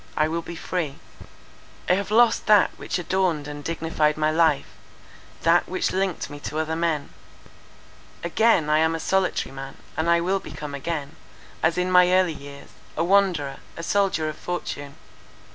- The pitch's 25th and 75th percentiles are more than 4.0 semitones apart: No, average, 3.3 semitones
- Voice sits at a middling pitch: Yes, medium, 165 Hz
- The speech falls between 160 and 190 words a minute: Yes, average, 165 wpm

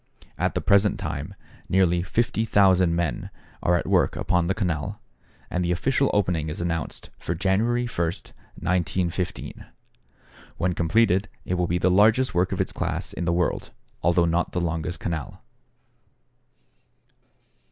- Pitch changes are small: Yes, narrow, 2.1 semitones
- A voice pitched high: No, very low, 90 Hz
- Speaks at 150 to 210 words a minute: No, average, 140 wpm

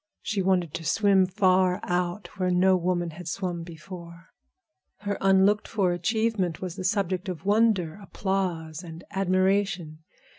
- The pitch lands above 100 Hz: Yes, medium, 185 Hz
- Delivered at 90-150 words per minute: Yes, average, 140 wpm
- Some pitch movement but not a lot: No, narrow, 2.0 semitones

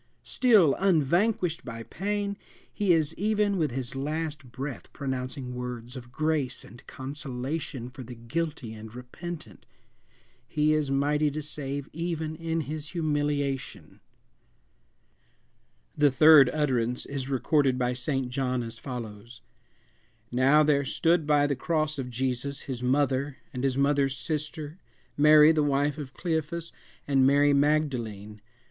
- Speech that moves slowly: Yes, slow, 130 wpm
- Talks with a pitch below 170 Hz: Yes, medium, 140 Hz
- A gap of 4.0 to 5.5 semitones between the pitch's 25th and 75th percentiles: No, average, 3.4 semitones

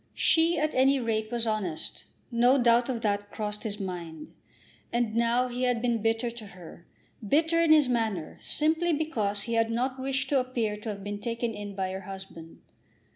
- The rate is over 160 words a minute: Yes, average, 185 wpm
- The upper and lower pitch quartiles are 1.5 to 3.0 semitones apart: No, average, 3.8 semitones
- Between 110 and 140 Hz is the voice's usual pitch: No, high, 230 Hz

